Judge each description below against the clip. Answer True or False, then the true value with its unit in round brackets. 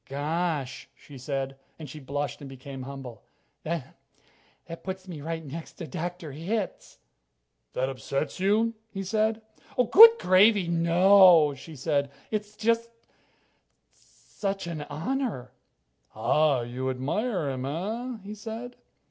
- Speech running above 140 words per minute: False (135 wpm)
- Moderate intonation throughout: False (6.4 semitones)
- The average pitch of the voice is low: False (165 Hz)